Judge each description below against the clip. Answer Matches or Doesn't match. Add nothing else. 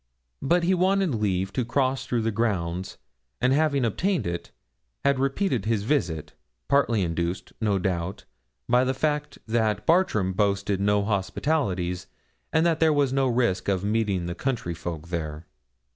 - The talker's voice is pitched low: Matches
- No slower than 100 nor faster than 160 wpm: Matches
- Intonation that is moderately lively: Doesn't match